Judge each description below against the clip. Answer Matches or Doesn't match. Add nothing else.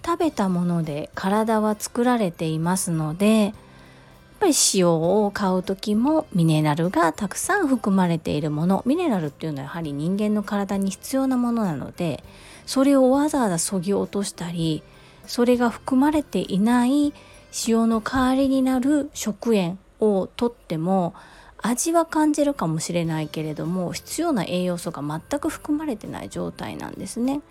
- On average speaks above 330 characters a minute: Doesn't match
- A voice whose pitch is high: Matches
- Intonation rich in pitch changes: Matches